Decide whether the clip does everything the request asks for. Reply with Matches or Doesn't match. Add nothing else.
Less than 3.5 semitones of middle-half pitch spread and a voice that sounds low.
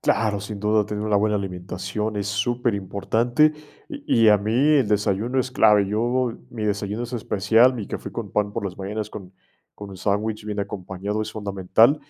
Matches